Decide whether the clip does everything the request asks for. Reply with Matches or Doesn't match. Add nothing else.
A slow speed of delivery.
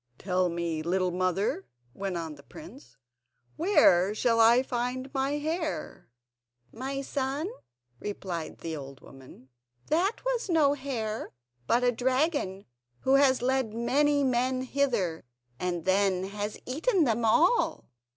Matches